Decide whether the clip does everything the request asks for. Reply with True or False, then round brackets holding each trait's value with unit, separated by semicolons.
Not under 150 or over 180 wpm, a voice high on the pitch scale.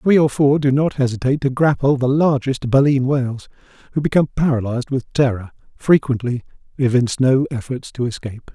False (155 wpm; 135 Hz)